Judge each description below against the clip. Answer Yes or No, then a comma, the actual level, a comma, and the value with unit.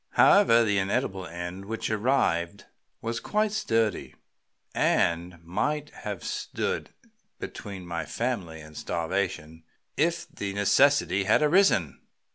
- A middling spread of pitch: No, wide, 6.5 semitones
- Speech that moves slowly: Yes, slow, 110 wpm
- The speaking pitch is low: Yes, low, 100 Hz